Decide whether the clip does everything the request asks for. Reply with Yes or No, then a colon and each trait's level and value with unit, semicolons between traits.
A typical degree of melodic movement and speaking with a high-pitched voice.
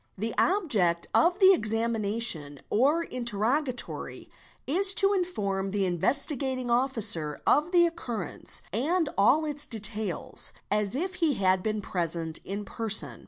No: wide, 7.3 semitones; high, 230 Hz